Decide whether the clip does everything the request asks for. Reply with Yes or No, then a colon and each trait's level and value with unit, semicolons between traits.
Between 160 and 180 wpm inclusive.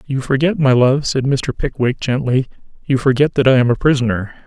No: average, 200 wpm